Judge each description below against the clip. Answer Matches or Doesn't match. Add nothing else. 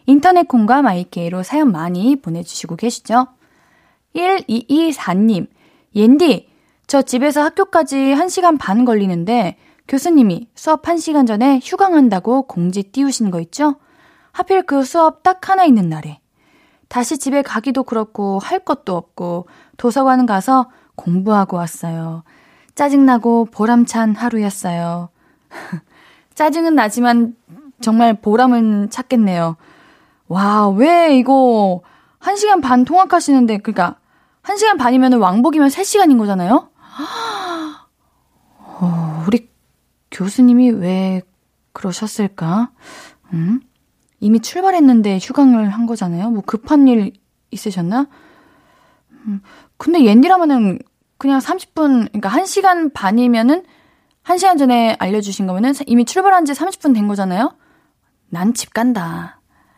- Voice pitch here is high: Matches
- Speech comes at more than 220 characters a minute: Matches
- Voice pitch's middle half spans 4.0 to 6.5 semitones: Doesn't match